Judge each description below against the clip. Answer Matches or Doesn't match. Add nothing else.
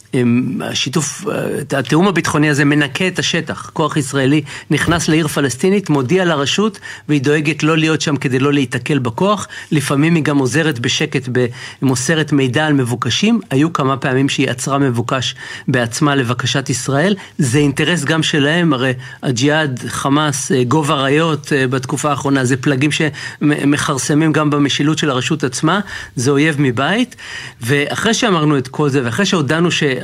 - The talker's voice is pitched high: Doesn't match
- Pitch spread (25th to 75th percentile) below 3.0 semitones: Matches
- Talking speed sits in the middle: Matches